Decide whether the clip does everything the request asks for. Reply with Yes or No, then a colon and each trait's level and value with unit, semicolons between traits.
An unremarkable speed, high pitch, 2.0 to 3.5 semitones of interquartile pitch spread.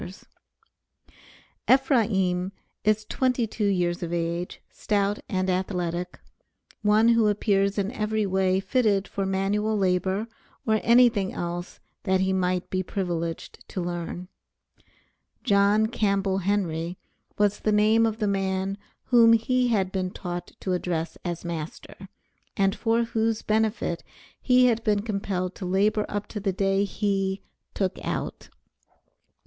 No: slow, 130 wpm; high, 195 Hz; average, 2.7 semitones